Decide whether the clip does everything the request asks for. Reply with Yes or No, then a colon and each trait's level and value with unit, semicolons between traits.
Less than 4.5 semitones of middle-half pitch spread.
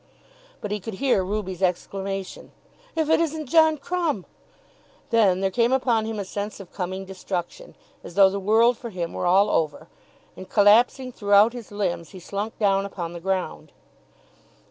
Yes: average, 3.7 semitones